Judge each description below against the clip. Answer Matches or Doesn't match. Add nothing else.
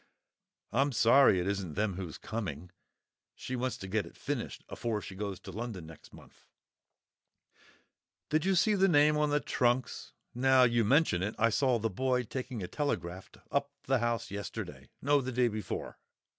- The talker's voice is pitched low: Matches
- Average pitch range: Matches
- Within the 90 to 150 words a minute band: Doesn't match